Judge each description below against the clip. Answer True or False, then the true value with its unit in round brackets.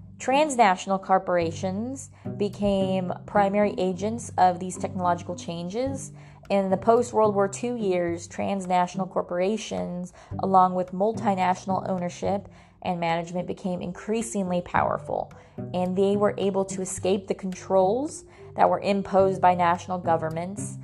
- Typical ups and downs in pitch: False (2.0 semitones)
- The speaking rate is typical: False (120 wpm)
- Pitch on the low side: False (190 Hz)